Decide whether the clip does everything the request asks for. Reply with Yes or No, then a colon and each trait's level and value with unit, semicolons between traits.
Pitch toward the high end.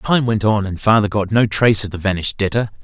No: low, 105 Hz